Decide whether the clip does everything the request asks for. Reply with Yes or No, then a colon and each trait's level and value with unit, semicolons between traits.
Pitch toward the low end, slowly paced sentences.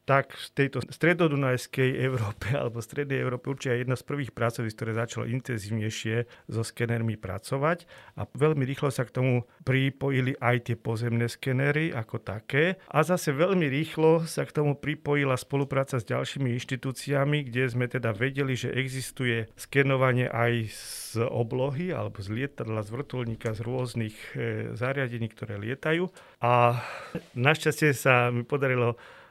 No: low, 130 Hz; average, 140 wpm